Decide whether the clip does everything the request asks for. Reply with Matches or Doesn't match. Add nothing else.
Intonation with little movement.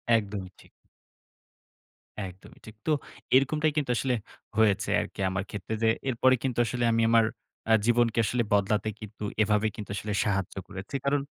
Doesn't match